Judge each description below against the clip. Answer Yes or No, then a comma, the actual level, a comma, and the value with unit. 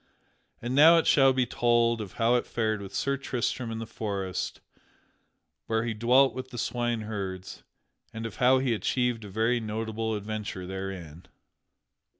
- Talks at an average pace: Yes, average, 155 wpm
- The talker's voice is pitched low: Yes, low, 115 Hz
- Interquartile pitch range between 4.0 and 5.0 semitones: No, narrow, 2.6 semitones